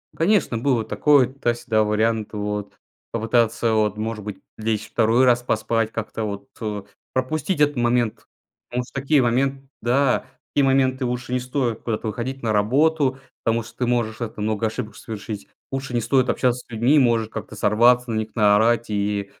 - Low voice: Yes, low, 115 Hz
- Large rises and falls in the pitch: No, average, 2.9 semitones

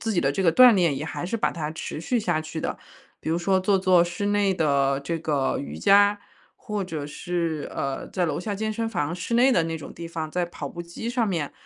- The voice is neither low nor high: Yes, medium, 175 Hz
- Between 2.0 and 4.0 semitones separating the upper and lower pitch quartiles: No, average, 4.4 semitones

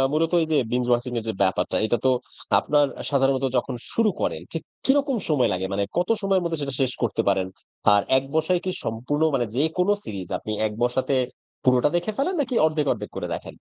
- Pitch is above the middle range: No, low, 135 Hz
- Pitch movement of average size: No, wide, 5.9 semitones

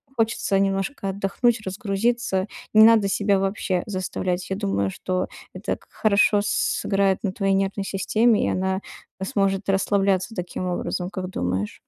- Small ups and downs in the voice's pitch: Yes, narrow, 1.6 semitones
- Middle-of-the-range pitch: No, high, 195 Hz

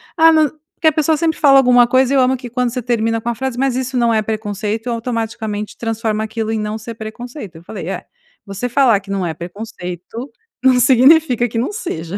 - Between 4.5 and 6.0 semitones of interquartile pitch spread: No, average, 3.3 semitones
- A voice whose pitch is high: Yes, high, 235 Hz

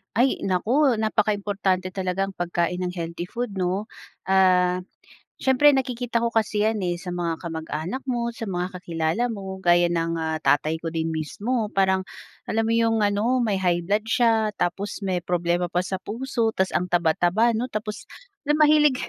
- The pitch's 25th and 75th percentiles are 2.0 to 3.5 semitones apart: No, average, 4.3 semitones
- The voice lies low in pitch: No, high, 190 Hz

